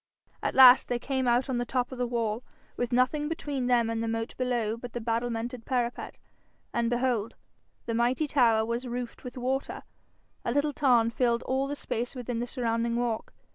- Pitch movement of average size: No, narrow, 1.7 semitones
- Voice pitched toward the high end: Yes, high, 245 Hz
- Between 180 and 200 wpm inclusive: Yes, average, 190 wpm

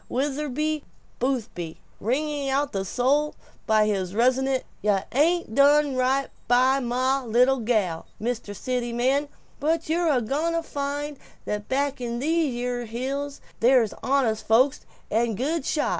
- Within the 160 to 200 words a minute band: No, average, 140 wpm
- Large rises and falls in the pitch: No, average, 3.5 semitones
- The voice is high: Yes, very high, 260 Hz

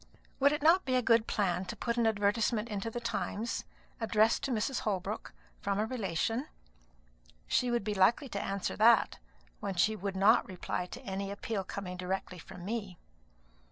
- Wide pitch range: No, average, 3.4 semitones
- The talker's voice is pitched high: Yes, high, 210 Hz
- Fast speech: No, average, 175 wpm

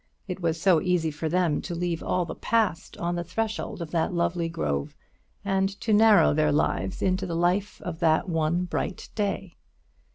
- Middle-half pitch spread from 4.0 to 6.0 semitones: No, narrow, 2.6 semitones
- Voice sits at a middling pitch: Yes, medium, 175 Hz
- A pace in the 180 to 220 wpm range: Yes, average, 185 wpm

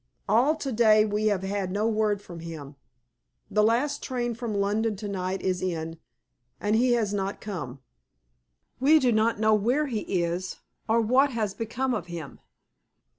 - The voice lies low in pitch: No, high, 215 Hz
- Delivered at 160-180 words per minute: Yes, average, 170 wpm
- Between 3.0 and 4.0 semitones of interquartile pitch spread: Yes, average, 3.6 semitones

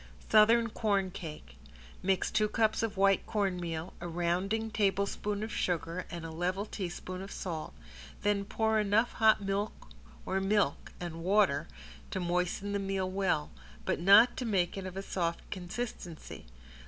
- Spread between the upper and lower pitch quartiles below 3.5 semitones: Yes, average, 3.0 semitones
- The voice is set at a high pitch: Yes, high, 195 Hz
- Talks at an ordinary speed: Yes, average, 150 wpm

